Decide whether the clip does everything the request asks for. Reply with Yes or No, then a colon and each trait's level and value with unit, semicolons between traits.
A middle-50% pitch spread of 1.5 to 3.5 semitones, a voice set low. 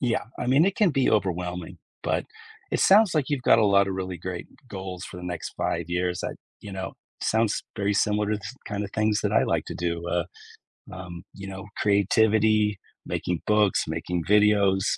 Yes: average, 3.1 semitones; low, 100 Hz